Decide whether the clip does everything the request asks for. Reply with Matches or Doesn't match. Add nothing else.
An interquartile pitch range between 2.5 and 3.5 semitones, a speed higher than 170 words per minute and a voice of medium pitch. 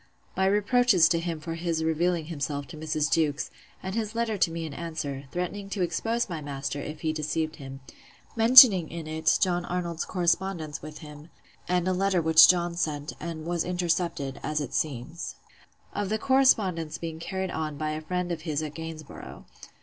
Matches